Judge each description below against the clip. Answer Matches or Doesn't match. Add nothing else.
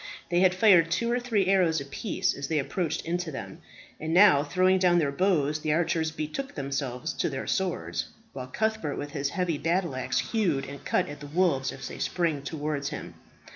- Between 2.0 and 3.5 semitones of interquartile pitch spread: Doesn't match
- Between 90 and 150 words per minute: Doesn't match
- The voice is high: Doesn't match